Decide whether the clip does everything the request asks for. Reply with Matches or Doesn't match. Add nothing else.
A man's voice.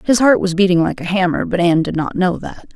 Doesn't match